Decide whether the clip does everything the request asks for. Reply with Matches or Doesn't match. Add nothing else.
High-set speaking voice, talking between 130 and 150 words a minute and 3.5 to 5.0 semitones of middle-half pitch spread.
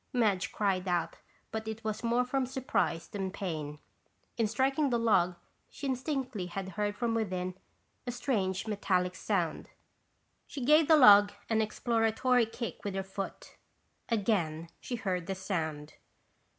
Matches